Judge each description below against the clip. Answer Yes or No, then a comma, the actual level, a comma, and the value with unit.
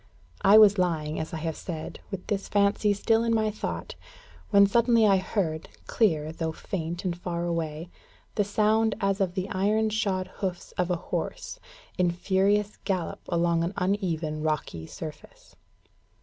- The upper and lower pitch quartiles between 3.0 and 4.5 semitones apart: Yes, average, 3.7 semitones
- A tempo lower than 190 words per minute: Yes, average, 160 wpm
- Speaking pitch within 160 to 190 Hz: Yes, medium, 185 Hz